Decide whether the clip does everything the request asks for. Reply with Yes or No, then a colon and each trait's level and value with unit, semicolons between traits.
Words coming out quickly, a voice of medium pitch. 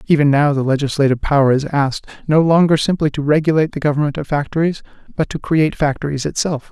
No: average, 190 wpm; medium, 150 Hz